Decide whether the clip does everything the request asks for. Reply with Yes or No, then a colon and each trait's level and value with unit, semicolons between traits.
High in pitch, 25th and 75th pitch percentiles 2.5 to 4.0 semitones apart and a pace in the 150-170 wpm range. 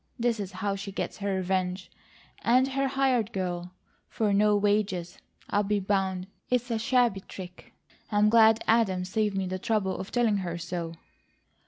Yes: high, 200 Hz; average, 3.1 semitones; average, 165 wpm